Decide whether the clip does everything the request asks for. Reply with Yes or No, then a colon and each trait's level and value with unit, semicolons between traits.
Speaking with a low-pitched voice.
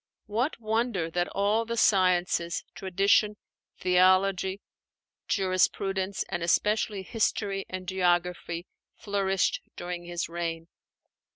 No: high, 190 Hz